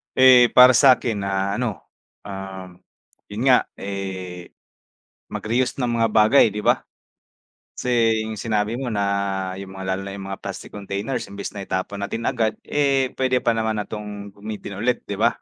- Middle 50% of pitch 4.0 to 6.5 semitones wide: No, average, 3.4 semitones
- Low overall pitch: Yes, low, 105 Hz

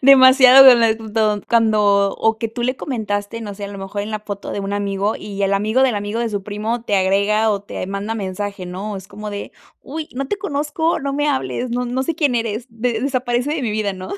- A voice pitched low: No, high, 220 Hz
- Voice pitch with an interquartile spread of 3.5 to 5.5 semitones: Yes, average, 3.9 semitones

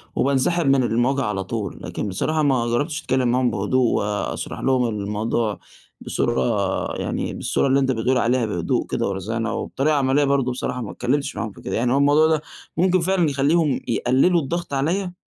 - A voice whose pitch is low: Yes, low, 130 Hz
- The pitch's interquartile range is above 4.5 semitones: No, average, 4.1 semitones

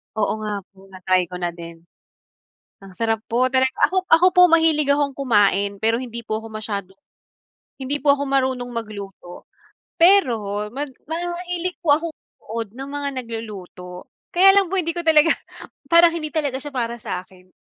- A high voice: Yes, very high, 250 Hz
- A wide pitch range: Yes, wide, 7.2 semitones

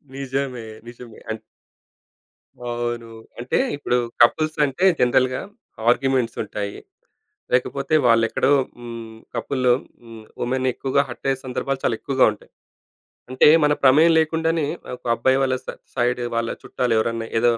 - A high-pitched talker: No, low, 125 Hz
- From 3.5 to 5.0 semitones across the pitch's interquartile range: No, narrow, 2.6 semitones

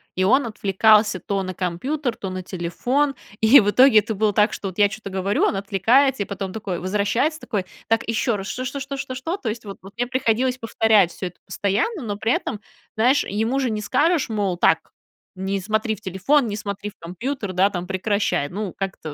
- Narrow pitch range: No, average, 4.2 semitones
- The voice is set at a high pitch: Yes, high, 210 Hz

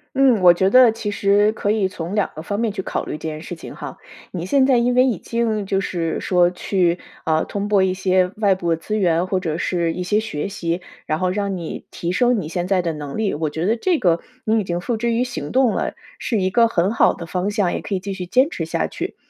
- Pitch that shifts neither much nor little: Yes, average, 3.9 semitones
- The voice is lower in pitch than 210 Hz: Yes, high, 190 Hz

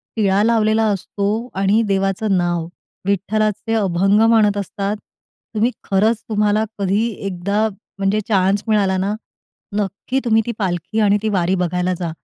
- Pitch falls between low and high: No, high, 200 Hz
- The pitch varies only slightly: Yes, narrow, 2.2 semitones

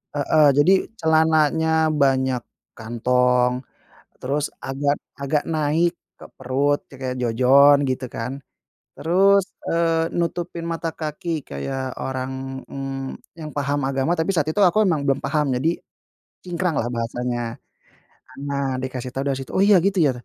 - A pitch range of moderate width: Yes, average, 3.7 semitones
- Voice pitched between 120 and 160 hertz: Yes, medium, 140 Hz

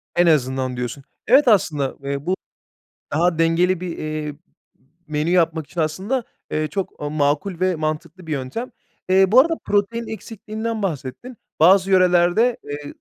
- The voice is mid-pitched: Yes, medium, 175 Hz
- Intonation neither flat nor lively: Yes, average, 4.7 semitones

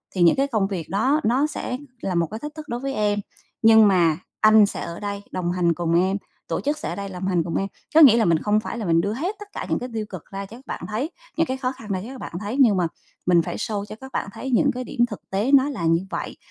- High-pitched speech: Yes, high, 210 Hz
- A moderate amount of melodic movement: No, wide, 5.7 semitones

